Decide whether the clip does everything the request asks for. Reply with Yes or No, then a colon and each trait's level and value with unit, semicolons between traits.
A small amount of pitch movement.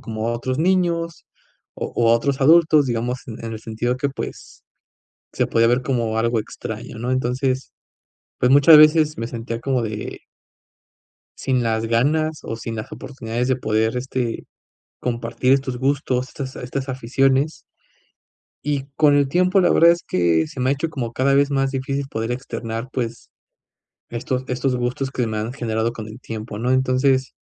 No: average, 3.1 semitones